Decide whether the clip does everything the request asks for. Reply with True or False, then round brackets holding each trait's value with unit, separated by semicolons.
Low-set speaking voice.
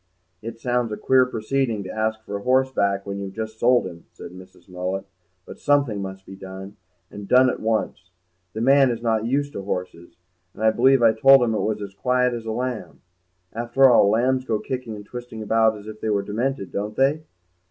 True (110 Hz)